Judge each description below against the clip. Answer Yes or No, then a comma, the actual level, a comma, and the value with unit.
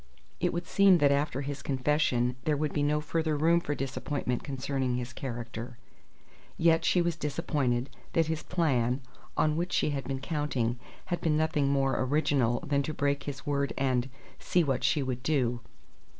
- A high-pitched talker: No, medium, 140 Hz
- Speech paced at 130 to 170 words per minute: No, average, 180 wpm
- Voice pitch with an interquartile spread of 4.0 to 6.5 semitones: No, average, 3.1 semitones